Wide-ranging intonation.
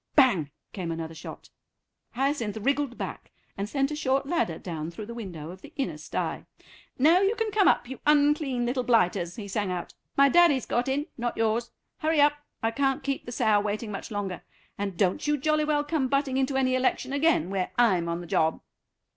Yes: wide, 6.3 semitones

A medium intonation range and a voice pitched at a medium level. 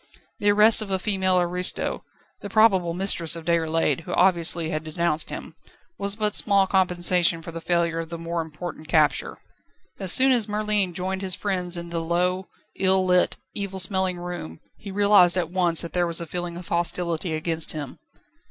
No: narrow, 2.2 semitones; medium, 180 Hz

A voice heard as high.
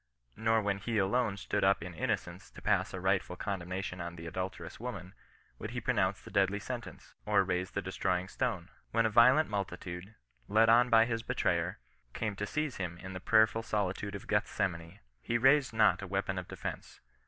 No: low, 100 Hz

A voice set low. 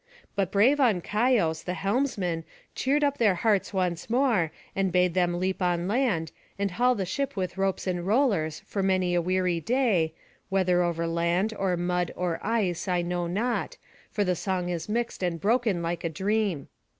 No: medium, 185 Hz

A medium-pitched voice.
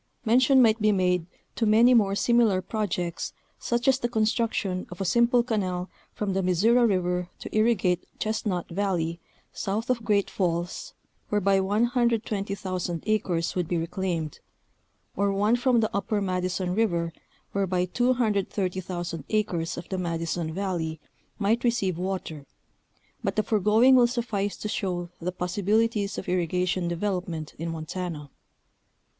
No: high, 195 Hz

